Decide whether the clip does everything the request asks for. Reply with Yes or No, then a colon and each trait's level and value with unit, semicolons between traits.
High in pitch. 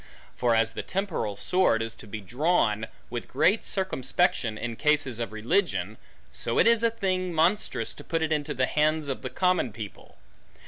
No: medium, 145 Hz